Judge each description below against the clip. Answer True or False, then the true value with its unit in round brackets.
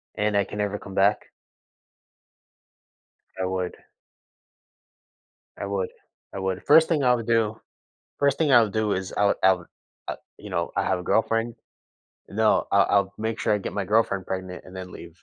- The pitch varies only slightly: False (3.0 semitones)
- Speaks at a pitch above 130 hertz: False (100 Hz)